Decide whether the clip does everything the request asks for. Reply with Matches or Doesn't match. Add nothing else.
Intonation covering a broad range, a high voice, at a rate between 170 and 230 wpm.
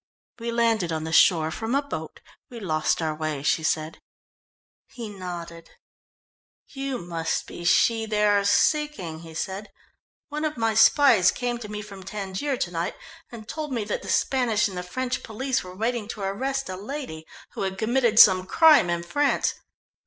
Matches